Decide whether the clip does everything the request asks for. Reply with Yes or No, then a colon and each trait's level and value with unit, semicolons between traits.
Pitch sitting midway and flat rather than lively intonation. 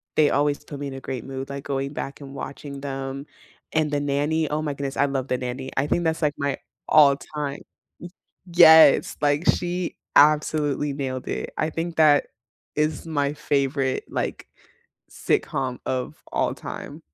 Yes: medium, 145 Hz; narrow, 1.9 semitones